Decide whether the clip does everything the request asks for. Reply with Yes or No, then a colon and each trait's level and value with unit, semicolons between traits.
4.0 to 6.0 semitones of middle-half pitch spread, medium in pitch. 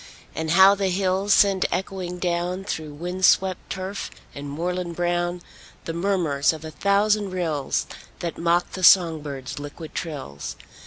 No: average, 2.9 semitones; medium, 175 Hz